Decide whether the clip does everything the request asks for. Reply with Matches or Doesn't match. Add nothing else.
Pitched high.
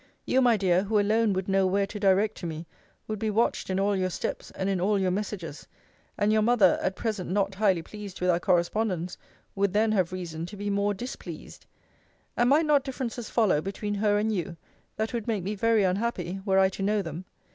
Matches